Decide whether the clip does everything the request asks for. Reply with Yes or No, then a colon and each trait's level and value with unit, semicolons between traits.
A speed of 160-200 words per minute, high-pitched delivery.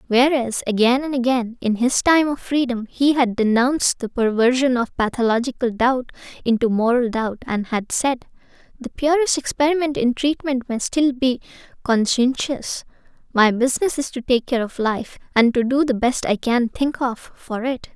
Yes: average, 165 wpm; very high, 250 Hz